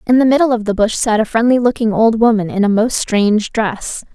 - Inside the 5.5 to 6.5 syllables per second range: Yes, 5.6 syllables/s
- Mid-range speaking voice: No, high, 225 Hz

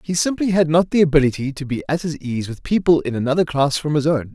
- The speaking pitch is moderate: Yes, medium, 150 Hz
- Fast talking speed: Yes, fast, 260 wpm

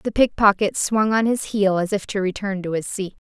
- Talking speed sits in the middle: No, fast, 240 wpm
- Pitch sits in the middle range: No, high, 200 Hz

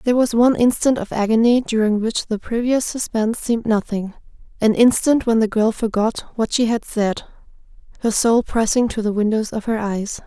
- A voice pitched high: Yes, high, 225 Hz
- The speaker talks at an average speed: Yes, average, 180 wpm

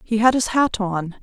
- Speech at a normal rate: No, fast, 245 wpm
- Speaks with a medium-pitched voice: No, high, 215 Hz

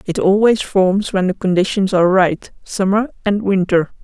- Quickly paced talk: No, average, 165 wpm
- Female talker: Yes, female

